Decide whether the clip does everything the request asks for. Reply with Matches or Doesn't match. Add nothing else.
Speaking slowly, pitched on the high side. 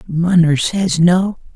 Doesn't match